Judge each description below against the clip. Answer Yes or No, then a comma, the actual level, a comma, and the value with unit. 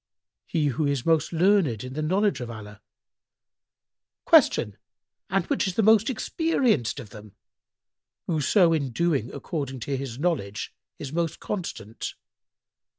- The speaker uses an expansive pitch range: Yes, wide, 6.7 semitones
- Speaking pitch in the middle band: Yes, medium, 150 Hz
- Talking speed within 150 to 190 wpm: No, slow, 135 wpm